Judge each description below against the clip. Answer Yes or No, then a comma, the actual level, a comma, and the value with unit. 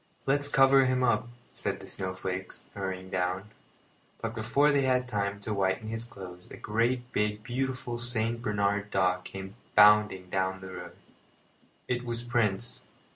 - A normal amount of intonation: Yes, average, 4.3 semitones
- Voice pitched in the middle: No, low, 105 Hz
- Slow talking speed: No, average, 150 wpm